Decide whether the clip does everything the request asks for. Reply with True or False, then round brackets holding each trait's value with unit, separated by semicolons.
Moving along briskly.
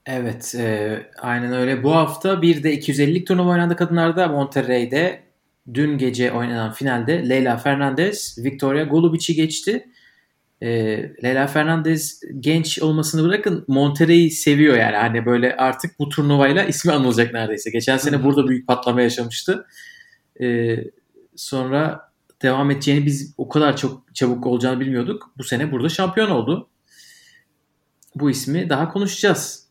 False (130 wpm)